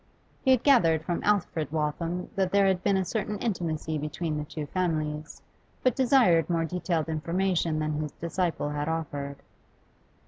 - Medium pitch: Yes, medium, 165 Hz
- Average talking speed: Yes, average, 160 wpm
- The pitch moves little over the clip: No, average, 3.7 semitones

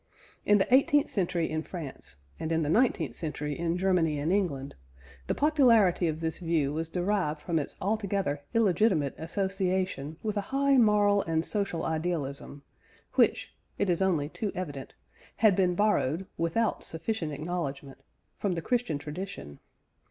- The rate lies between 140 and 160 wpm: Yes, average, 150 wpm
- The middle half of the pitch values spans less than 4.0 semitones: No, average, 4.7 semitones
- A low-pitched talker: No, medium, 175 Hz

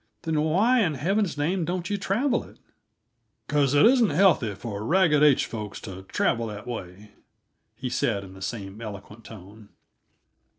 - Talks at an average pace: Yes, average, 160 wpm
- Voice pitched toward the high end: No, low, 130 Hz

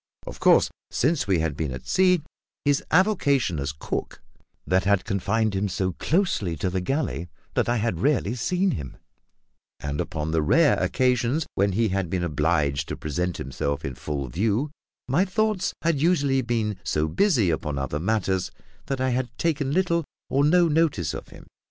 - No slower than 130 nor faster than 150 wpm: No, average, 170 wpm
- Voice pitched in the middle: No, low, 110 Hz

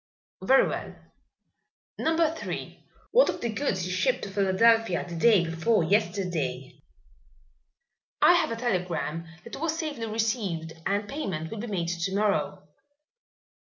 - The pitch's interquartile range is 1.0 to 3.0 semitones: No, average, 5.2 semitones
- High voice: Yes, high, 200 Hz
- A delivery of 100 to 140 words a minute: Yes, slow, 135 wpm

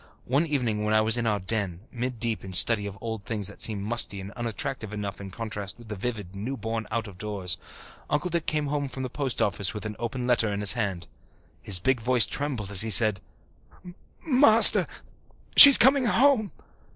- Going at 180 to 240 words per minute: Yes, average, 200 wpm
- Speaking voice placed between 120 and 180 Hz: No, low, 110 Hz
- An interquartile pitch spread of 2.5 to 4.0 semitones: No, average, 4.4 semitones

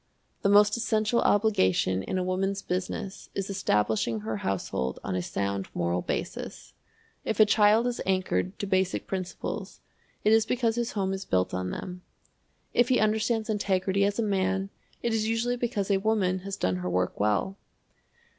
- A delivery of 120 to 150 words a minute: No, average, 170 wpm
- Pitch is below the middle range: No, high, 195 Hz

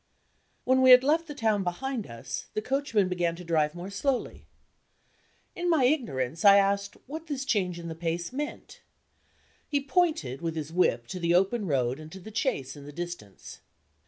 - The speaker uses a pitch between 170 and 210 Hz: Yes, high, 190 Hz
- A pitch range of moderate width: No, wide, 8.0 semitones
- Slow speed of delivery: No, average, 185 wpm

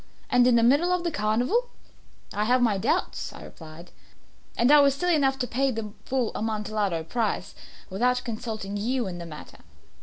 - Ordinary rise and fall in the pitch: Yes, average, 4.3 semitones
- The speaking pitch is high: Yes, high, 235 Hz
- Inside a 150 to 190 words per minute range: Yes, average, 180 wpm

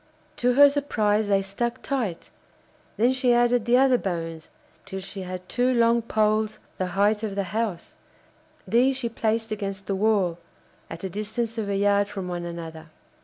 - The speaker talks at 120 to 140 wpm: No, average, 170 wpm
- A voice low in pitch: No, high, 210 Hz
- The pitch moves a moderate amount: Yes, average, 3.7 semitones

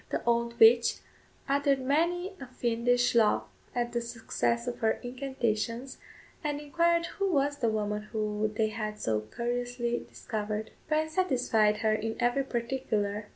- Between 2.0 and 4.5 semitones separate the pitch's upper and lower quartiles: Yes, average, 3.8 semitones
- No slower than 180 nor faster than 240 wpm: No, average, 145 wpm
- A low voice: No, high, 240 Hz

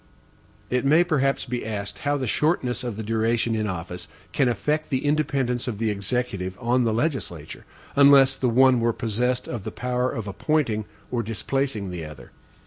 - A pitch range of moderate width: Yes, average, 3.9 semitones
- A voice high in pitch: No, low, 120 Hz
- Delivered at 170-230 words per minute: Yes, average, 175 wpm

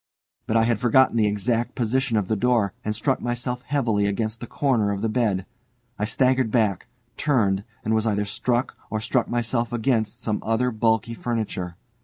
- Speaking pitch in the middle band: No, low, 115 Hz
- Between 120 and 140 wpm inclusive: No, average, 180 wpm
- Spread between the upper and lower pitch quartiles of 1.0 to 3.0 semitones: Yes, narrow, 2.5 semitones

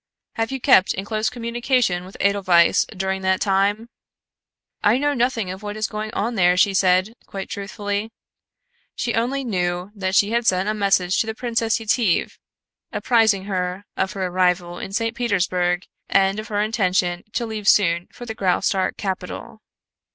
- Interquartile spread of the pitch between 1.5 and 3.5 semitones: Yes, average, 3.2 semitones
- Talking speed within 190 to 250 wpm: No, average, 165 wpm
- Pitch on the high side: Yes, high, 200 Hz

